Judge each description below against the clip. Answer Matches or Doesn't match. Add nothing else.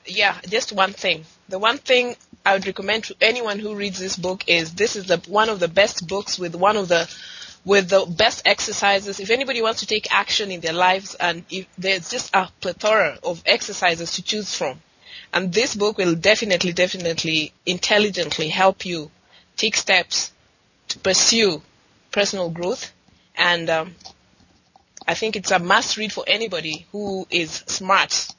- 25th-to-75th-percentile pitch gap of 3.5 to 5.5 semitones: Doesn't match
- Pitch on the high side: Matches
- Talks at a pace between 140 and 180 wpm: Matches